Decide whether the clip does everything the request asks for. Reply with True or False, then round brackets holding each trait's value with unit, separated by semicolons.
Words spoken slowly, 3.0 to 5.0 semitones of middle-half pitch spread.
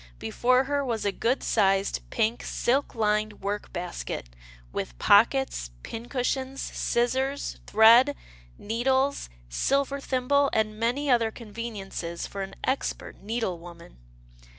True (115 wpm; 4.5 semitones)